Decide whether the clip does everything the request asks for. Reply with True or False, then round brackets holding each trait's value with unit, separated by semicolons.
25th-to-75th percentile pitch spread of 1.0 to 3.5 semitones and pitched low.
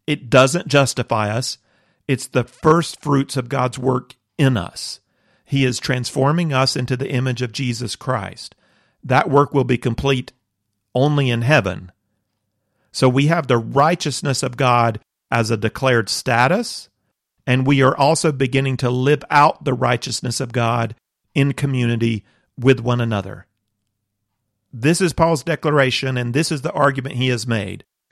True (2.9 semitones; 130 Hz)